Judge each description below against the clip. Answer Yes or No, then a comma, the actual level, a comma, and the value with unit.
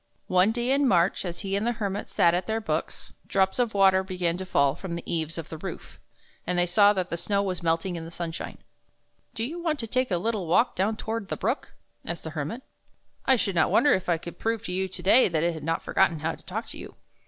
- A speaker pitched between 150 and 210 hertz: Yes, high, 190 Hz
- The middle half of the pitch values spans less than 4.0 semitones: No, average, 4.6 semitones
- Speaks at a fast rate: Yes, fast, 265 wpm